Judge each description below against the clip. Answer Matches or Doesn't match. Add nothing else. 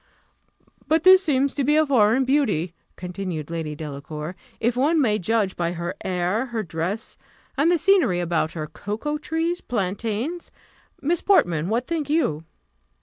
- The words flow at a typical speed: Matches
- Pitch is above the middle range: Matches